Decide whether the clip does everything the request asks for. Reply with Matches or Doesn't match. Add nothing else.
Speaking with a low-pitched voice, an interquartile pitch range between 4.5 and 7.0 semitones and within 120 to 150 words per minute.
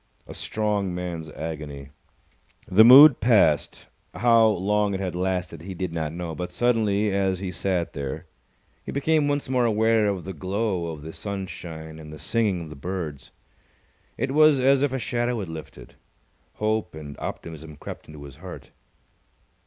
Doesn't match